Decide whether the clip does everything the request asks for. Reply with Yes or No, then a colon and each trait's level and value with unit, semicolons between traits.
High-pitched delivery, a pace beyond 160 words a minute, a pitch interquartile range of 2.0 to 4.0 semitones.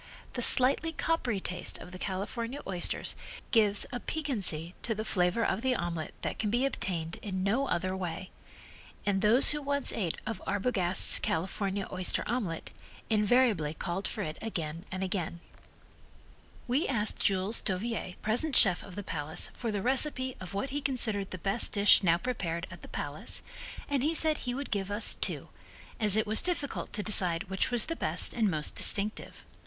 No: high, 205 Hz; average, 180 wpm; average, 5.0 semitones